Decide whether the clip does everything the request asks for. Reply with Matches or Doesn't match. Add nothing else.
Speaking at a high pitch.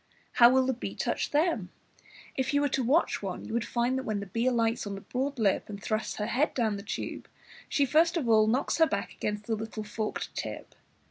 Matches